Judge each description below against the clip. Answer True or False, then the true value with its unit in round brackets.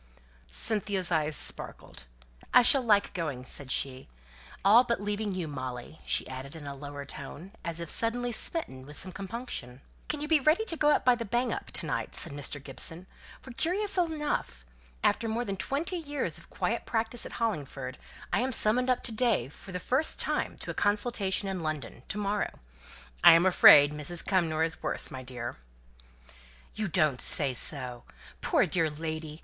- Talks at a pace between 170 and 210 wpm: True (175 wpm)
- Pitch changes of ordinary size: False (8.6 semitones)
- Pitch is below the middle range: False (185 Hz)